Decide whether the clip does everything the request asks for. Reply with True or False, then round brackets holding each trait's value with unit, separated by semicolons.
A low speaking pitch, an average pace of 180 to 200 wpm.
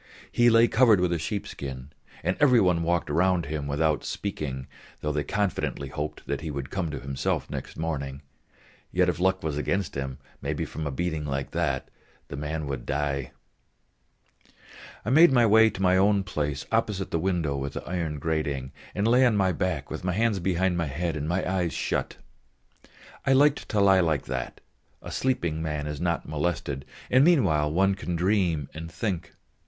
True (85 Hz; 185 wpm)